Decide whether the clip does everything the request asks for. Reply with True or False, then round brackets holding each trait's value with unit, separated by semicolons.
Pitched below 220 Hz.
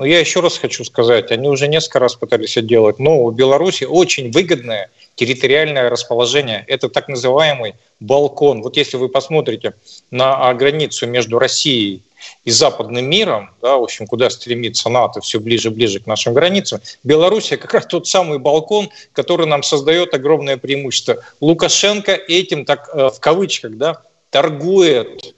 True (140 Hz)